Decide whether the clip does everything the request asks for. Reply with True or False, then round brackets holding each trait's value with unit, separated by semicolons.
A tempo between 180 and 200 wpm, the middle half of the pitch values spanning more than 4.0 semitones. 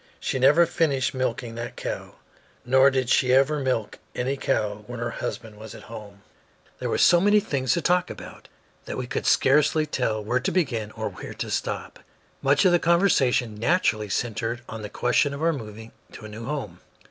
True (195 wpm; 4.8 semitones)